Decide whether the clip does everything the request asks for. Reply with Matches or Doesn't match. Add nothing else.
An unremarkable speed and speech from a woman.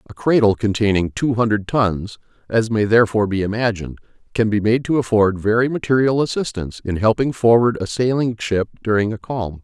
Doesn't match